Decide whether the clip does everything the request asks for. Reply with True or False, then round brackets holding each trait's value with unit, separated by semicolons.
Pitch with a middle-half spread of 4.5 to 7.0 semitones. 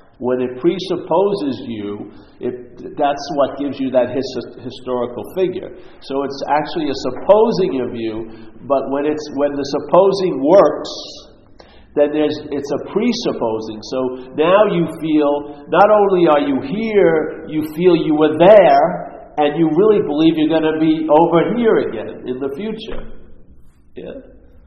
True (5.0 semitones)